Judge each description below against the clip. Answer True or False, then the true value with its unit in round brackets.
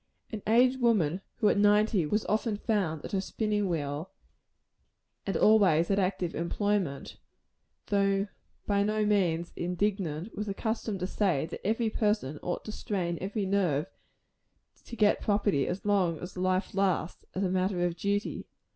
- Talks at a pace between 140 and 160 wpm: True (155 wpm)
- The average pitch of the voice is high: True (195 Hz)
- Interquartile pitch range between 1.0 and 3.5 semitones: True (3.0 semitones)